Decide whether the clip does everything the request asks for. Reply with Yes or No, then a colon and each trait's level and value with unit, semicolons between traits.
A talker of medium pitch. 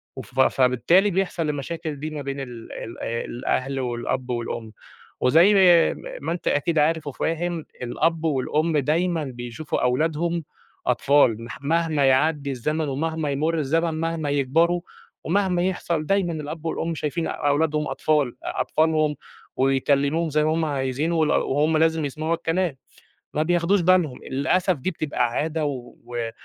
Yes: medium, 155 Hz